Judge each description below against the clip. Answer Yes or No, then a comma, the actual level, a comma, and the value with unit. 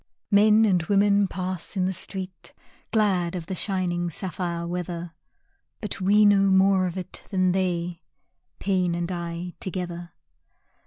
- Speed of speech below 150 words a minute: Yes, average, 140 wpm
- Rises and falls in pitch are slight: Yes, narrow, 2.1 semitones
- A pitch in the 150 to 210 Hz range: Yes, medium, 185 Hz